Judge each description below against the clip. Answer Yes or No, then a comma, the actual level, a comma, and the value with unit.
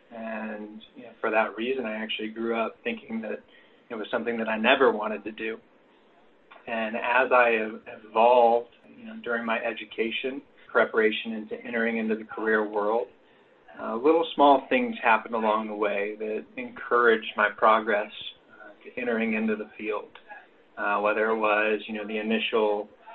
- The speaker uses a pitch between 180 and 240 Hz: No, low, 110 Hz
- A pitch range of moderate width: No, narrow, 2.0 semitones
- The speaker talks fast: No, average, 165 wpm